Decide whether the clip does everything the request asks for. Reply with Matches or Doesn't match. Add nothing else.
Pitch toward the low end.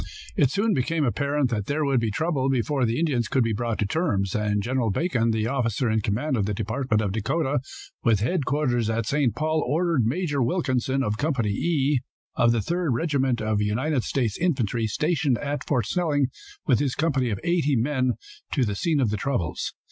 Matches